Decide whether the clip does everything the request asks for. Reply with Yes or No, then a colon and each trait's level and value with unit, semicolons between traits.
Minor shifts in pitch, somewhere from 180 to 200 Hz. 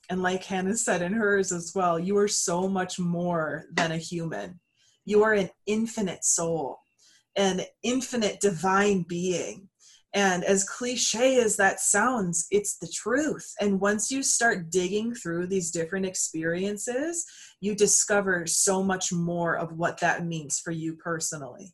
No: average, 3.1 semitones; high, 190 Hz